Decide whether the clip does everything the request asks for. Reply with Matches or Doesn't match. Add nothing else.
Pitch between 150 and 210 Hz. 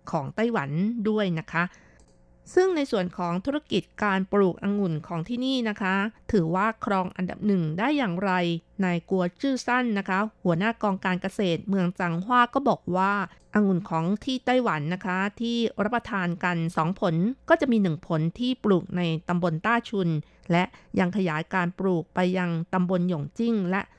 Matches